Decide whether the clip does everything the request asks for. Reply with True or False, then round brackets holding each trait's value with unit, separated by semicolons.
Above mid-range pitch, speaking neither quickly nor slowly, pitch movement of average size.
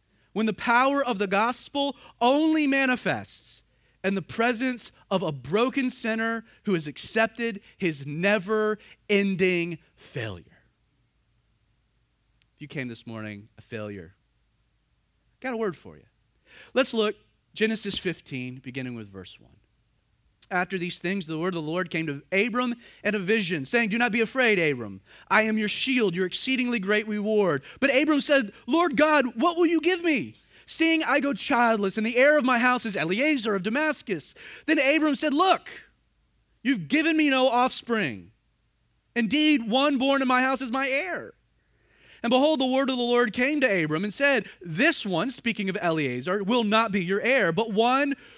False (220 Hz; 170 wpm; 7.5 semitones)